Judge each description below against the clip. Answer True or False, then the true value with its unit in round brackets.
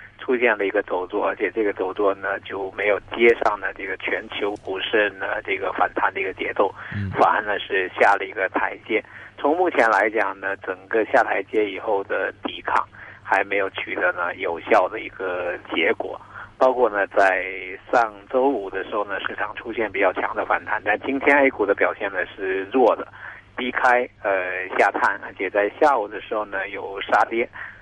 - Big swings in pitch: False (4.5 semitones)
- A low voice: True (120 Hz)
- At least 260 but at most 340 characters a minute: True (270 characters per minute)